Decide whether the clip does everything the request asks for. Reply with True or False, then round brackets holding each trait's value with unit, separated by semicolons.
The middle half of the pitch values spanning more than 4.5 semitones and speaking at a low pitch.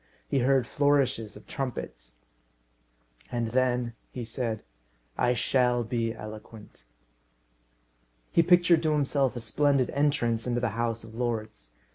False (3.2 semitones; 120 Hz)